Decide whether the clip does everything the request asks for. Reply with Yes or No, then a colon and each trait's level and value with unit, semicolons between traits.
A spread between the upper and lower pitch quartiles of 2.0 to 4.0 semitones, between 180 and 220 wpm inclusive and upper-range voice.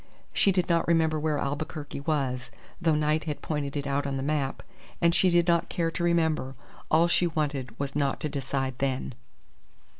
No: average, 3.1 semitones; average, 185 wpm; medium, 150 Hz